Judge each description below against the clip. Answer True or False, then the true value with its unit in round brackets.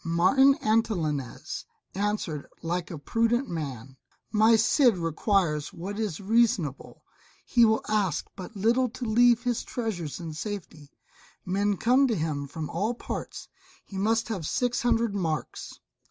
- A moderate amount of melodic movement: False (5.8 semitones)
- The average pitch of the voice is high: True (205 Hz)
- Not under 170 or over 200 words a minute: False (140 wpm)